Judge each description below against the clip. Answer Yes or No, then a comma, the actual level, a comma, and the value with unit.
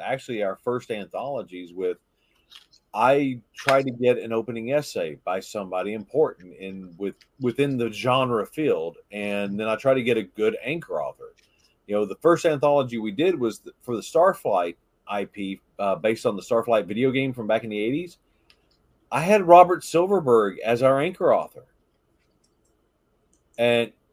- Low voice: Yes, low, 120 Hz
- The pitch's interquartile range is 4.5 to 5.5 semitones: Yes, average, 5.1 semitones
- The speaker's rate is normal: Yes, average, 160 wpm